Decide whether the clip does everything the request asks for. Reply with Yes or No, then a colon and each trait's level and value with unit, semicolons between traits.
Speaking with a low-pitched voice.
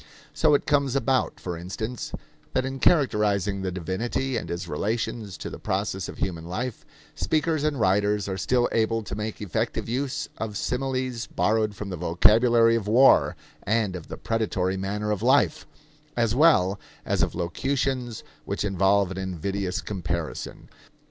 Yes: low, 105 Hz